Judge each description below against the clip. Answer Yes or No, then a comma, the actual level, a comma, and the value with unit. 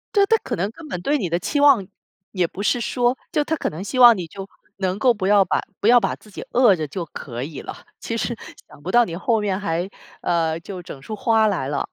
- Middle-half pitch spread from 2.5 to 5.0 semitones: No, wide, 5.6 semitones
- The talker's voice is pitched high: Yes, high, 200 Hz